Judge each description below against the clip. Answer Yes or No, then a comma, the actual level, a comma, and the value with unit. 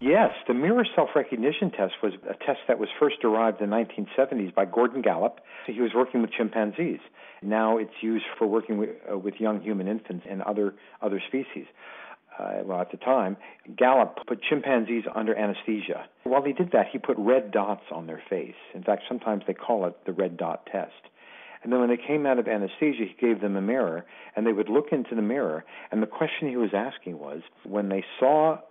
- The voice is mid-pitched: No, low, 110 Hz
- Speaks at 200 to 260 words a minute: Yes, fast, 205 wpm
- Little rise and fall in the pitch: No, average, 3.3 semitones